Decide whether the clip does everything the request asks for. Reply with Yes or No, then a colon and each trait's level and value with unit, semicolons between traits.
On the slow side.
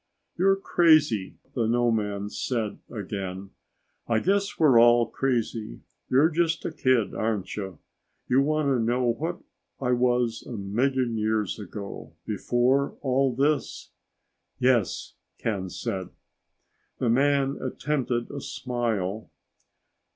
Yes: slow, 115 wpm